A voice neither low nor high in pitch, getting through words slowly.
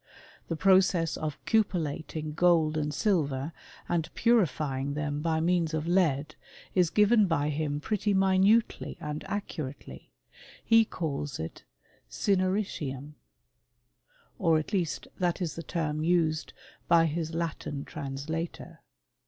Yes: medium, 160 Hz; slow, 120 wpm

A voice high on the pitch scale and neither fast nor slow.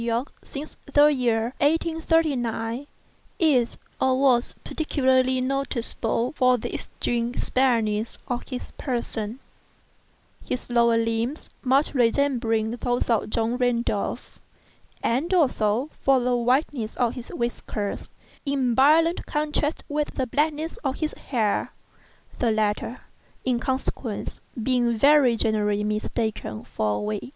No: very high, 250 Hz; slow, 115 wpm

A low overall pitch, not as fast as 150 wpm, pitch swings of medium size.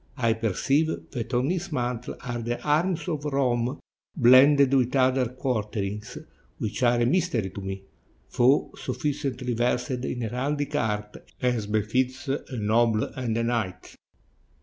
Yes: low, 125 Hz; average, 140 wpm; average, 3.4 semitones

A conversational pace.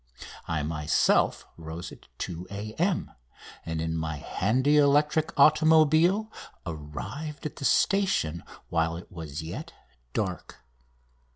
No: slow, 110 wpm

